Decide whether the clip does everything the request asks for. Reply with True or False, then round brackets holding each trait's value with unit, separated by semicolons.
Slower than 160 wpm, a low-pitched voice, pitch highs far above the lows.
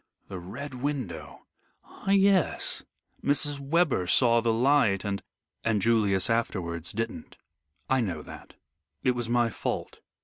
True (135 wpm; 115 Hz; 6.1 semitones)